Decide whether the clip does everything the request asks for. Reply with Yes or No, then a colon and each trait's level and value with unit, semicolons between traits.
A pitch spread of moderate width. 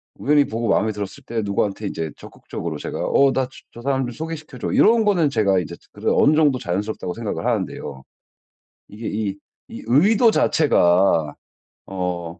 No: wide, 6.8 semitones